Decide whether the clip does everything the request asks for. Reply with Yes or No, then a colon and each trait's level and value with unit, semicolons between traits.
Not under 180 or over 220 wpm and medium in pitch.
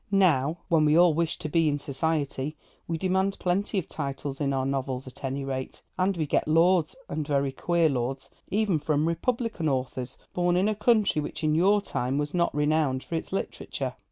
Yes: average, 195 wpm; medium, 155 Hz